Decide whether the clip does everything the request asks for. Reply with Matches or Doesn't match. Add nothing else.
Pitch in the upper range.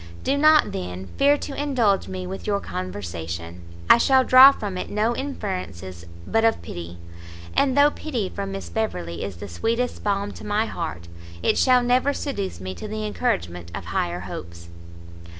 Matches